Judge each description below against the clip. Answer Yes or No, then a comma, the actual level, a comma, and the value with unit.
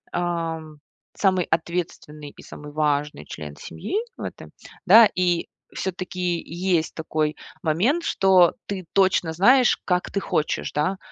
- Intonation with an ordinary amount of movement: Yes, average, 3.5 semitones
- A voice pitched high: No, medium, 175 Hz